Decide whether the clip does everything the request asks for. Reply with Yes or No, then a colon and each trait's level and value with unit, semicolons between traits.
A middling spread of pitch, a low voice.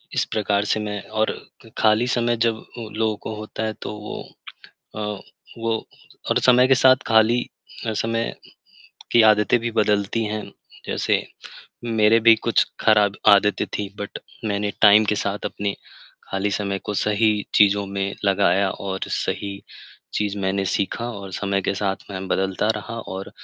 No: narrow, 1.9 semitones; low, 105 Hz